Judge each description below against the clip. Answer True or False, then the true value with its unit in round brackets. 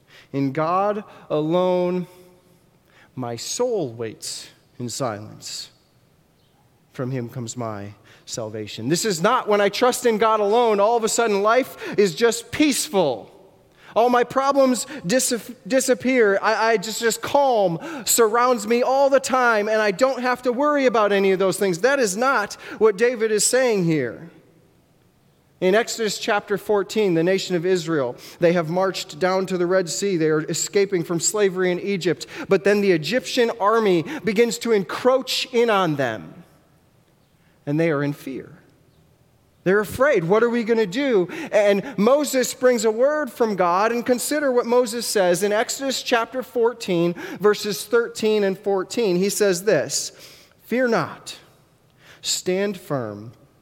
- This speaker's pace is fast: False (155 wpm)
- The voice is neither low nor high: False (205 Hz)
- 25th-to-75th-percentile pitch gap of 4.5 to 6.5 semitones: True (5.4 semitones)